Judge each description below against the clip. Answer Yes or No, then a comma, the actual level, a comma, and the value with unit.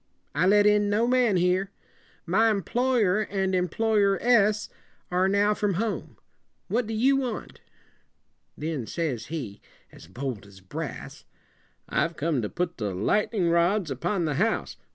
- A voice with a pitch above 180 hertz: Yes, high, 190 Hz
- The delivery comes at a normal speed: Yes, average, 165 wpm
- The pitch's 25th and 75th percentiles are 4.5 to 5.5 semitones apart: Yes, average, 5.1 semitones